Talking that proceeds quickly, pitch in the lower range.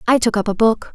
No: fast, 320 wpm; high, 225 Hz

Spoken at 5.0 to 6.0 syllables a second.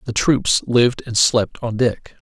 No: 4.0 syllables/s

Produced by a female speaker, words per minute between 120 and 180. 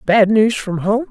No: female; fast, 220 wpm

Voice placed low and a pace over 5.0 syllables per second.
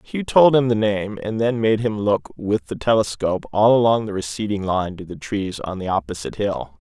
Yes: low, 105 Hz; 5.2 syllables/s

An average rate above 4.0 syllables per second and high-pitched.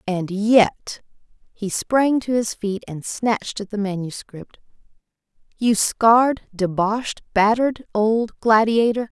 No: 3.6 syllables/s; high, 215 Hz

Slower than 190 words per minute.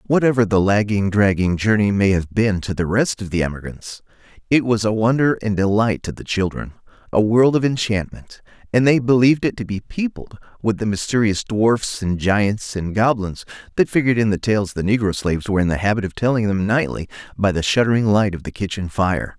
No: fast, 205 wpm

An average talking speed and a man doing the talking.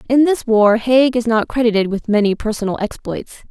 No: average, 190 wpm; female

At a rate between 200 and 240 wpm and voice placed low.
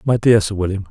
No: fast, 265 wpm; low, 100 Hz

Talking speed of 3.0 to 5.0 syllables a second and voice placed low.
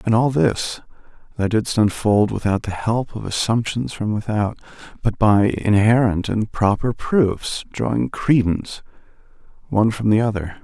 Yes: 4.4 syllables/s; low, 105 Hz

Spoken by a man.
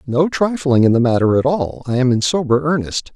Yes: male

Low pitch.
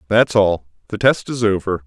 Yes: low, 100 Hz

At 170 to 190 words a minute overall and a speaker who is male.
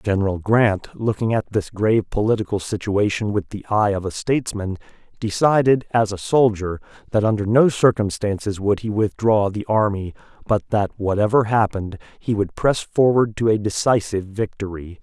No: average, 155 wpm; male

